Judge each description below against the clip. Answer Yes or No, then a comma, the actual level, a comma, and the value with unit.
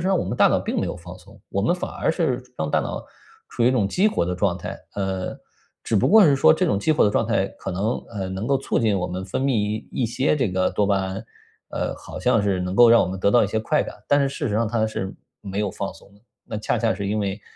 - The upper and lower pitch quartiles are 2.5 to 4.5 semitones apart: Yes, average, 3.6 semitones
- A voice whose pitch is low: Yes, low, 105 Hz